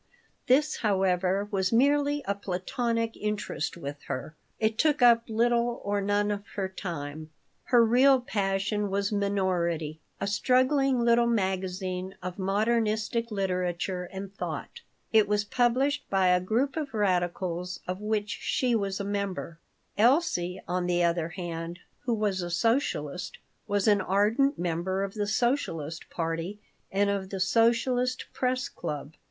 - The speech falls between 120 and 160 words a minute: Yes, average, 140 wpm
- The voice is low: No, high, 200 Hz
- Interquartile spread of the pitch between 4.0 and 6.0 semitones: Yes, average, 4.3 semitones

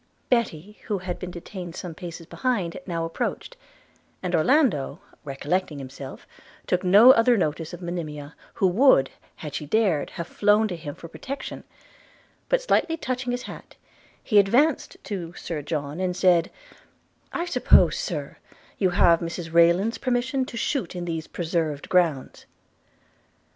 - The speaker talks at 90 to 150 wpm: Yes, average, 145 wpm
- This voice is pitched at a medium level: Yes, medium, 180 Hz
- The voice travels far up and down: Yes, wide, 5.7 semitones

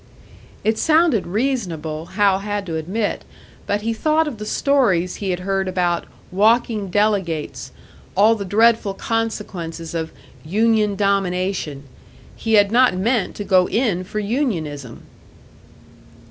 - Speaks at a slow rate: Yes, slow, 130 wpm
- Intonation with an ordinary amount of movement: Yes, average, 3.8 semitones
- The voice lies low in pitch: No, high, 200 Hz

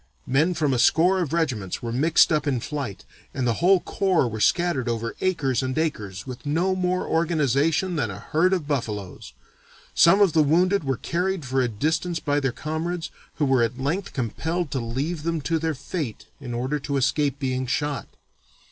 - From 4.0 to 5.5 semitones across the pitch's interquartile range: Yes, average, 4.7 semitones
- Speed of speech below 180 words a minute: No, average, 190 wpm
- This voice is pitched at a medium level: Yes, medium, 145 Hz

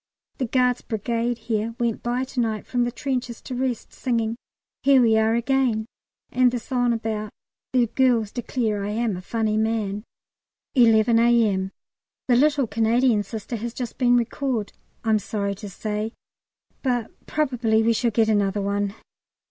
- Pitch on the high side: Yes, high, 230 Hz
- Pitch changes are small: Yes, narrow, 2.3 semitones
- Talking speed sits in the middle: Yes, average, 155 wpm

